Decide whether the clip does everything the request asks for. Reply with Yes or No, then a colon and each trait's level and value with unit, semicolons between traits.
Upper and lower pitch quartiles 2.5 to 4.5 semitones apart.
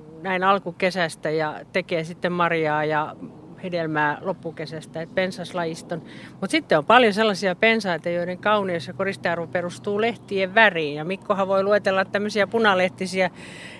Yes: average, 3.0 semitones